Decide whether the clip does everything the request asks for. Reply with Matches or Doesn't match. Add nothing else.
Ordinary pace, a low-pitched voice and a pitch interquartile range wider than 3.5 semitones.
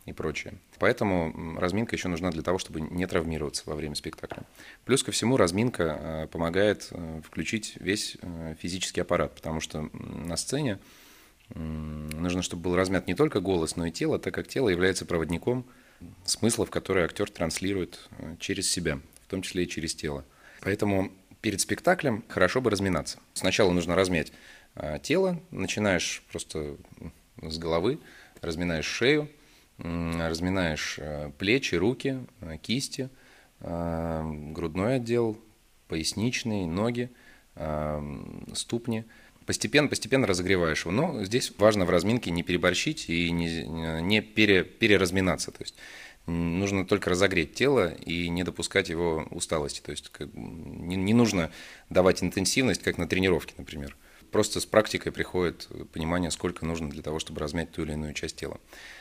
Matches